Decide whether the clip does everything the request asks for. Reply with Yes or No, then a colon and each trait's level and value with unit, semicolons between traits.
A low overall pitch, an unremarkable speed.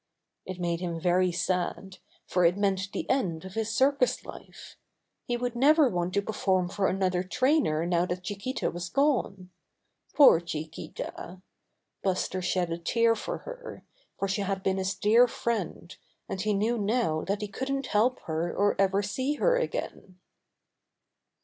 No: high, 195 Hz; average, 160 wpm